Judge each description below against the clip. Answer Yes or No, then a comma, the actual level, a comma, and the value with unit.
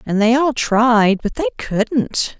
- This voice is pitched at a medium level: No, high, 240 Hz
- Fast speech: No, average, 175 wpm